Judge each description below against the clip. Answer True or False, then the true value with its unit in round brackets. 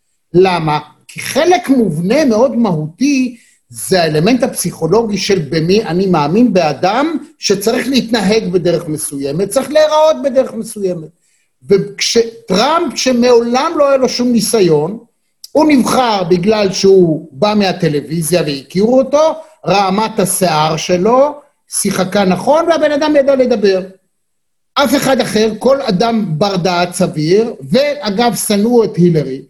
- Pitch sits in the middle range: False (210 Hz)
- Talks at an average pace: True (120 wpm)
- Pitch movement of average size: False (6.1 semitones)